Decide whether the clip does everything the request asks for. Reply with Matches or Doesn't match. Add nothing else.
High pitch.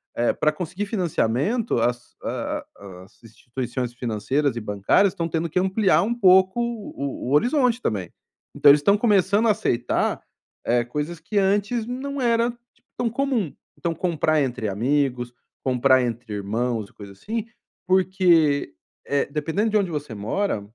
Doesn't match